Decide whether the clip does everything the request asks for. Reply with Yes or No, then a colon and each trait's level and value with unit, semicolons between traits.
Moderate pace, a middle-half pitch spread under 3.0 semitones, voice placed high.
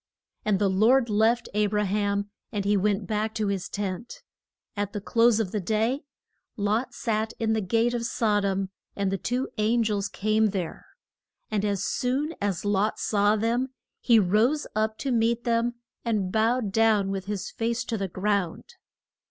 Yes: average, 175 wpm; narrow, 2.4 semitones; high, 215 Hz